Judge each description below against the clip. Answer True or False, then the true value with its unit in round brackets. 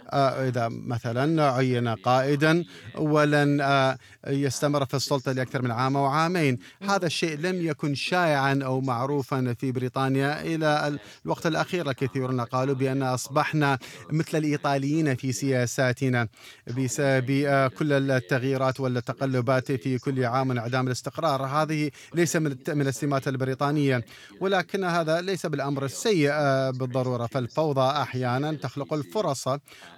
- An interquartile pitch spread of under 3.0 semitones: True (2.4 semitones)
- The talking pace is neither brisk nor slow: True (125 wpm)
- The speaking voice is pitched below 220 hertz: True (135 Hz)